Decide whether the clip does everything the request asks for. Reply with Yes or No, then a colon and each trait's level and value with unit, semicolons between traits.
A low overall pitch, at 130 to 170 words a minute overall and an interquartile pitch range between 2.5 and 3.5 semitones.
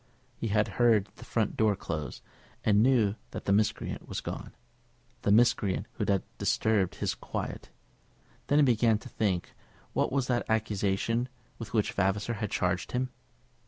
Yes: low, 105 Hz; average, 160 wpm; average, 2.9 semitones